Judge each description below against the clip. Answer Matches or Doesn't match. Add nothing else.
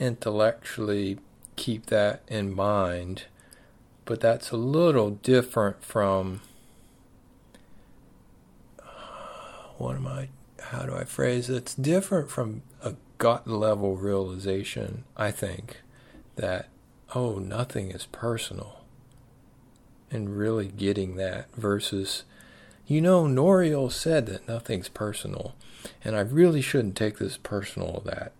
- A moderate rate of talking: Doesn't match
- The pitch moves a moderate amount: Matches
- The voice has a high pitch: Doesn't match